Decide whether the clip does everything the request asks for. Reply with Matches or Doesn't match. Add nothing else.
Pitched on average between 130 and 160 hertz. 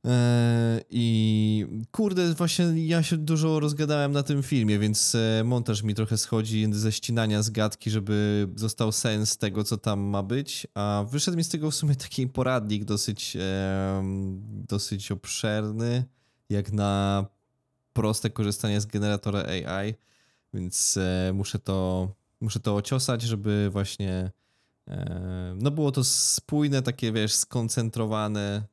Doesn't match